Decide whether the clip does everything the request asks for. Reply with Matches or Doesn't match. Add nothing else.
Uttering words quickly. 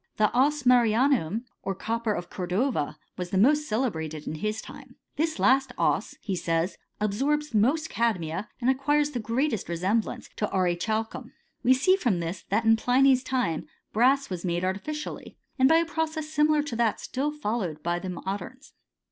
Doesn't match